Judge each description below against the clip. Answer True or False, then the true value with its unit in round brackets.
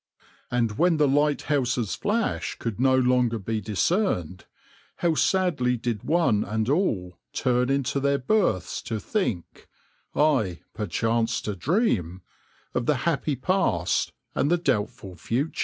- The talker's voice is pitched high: False (125 Hz)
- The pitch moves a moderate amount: False (5.9 semitones)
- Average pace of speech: False (130 wpm)